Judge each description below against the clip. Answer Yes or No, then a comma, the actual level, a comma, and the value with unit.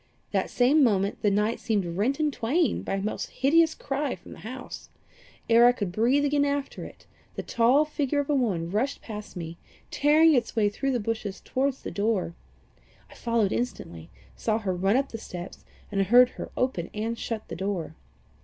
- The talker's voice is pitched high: Yes, high, 230 Hz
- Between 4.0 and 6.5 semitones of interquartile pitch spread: Yes, average, 5.3 semitones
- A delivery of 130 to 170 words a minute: No, average, 190 wpm